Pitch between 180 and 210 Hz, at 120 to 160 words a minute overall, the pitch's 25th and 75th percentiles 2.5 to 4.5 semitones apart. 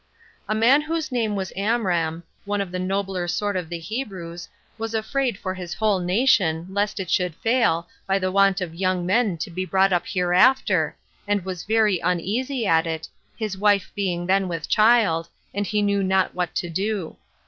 No: high, 190 Hz; average, 185 wpm; average, 3.4 semitones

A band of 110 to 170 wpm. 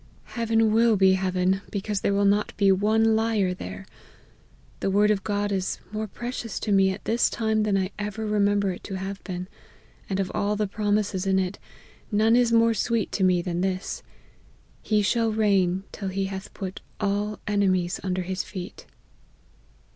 No: average, 185 wpm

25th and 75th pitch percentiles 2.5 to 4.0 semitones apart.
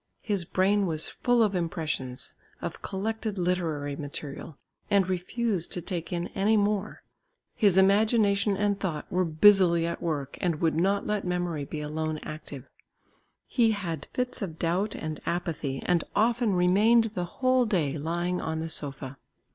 No: average, 4.5 semitones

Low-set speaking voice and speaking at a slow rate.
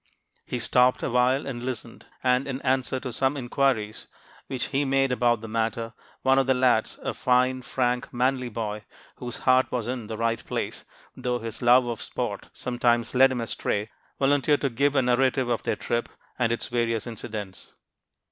No: low, 125 Hz; average, 175 wpm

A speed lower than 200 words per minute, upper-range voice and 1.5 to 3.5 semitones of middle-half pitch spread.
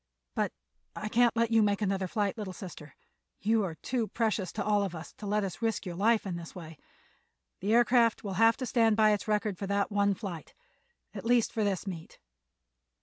No: fast, 205 wpm; high, 210 Hz; average, 2.9 semitones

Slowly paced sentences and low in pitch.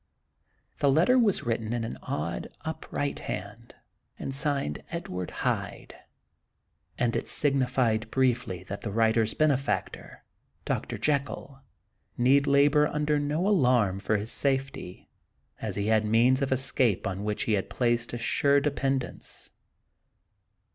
Yes: slow, 130 wpm; low, 125 Hz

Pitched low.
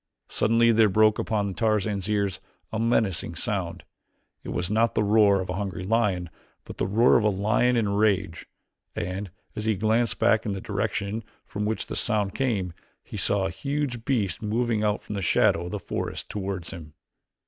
Yes: low, 105 Hz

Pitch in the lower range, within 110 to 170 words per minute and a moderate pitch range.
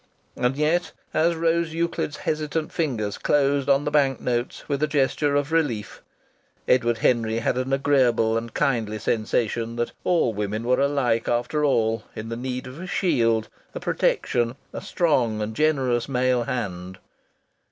Yes: low, 125 Hz; average, 155 wpm; average, 4.2 semitones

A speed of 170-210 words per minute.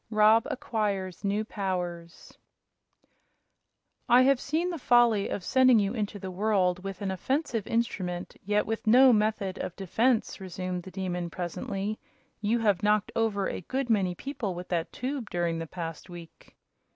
No: average, 155 wpm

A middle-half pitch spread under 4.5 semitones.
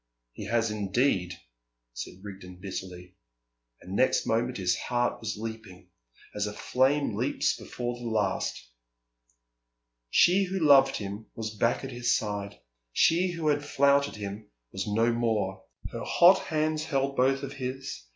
No: average, 5.3 semitones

